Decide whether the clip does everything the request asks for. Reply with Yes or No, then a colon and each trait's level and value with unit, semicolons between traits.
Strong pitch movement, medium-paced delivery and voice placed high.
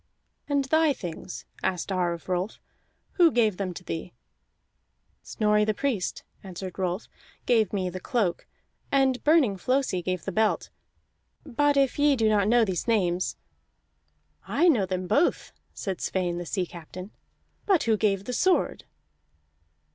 Yes: wide, 5.8 semitones; average, 150 wpm; high, 205 Hz